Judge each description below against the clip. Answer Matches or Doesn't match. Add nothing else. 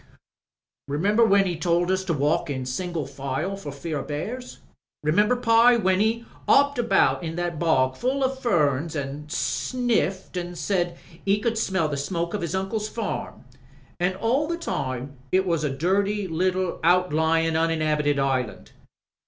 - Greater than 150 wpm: Matches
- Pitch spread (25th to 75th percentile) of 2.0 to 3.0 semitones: Doesn't match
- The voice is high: Doesn't match